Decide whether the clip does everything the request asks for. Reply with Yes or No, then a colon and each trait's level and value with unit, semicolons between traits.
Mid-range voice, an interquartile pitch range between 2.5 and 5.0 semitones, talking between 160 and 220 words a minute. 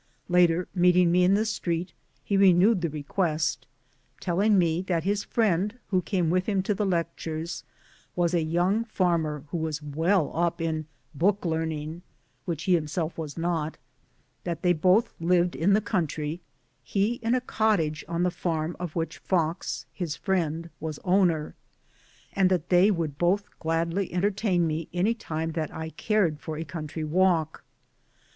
Yes: medium, 175 Hz; average, 2.9 semitones; average, 165 wpm